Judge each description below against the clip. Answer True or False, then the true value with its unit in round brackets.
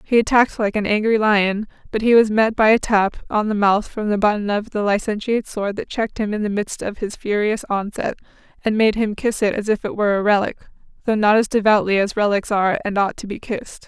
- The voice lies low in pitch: False (210 Hz)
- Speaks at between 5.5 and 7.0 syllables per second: True (5.9 syllables/s)